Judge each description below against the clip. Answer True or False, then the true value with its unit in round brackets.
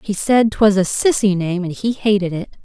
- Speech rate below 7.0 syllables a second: True (4.8 syllables/s)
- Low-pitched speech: False (200 Hz)